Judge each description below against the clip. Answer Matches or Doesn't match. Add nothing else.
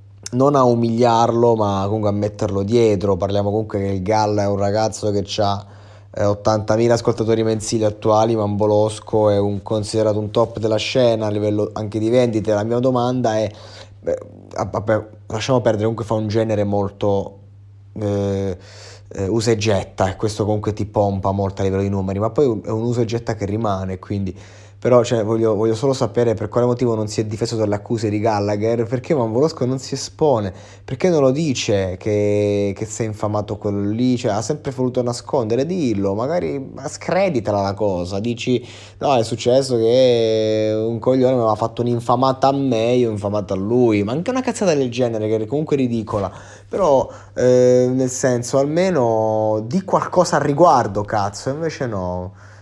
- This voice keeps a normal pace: Doesn't match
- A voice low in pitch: Matches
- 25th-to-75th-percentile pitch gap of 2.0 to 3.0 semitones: Matches